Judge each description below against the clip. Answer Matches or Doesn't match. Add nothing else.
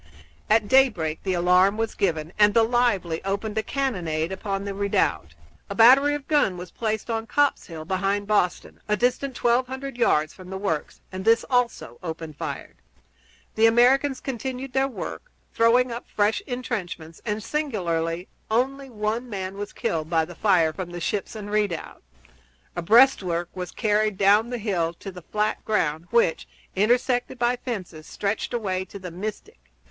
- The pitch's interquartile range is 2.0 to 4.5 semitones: Doesn't match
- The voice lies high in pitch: Matches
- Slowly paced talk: Doesn't match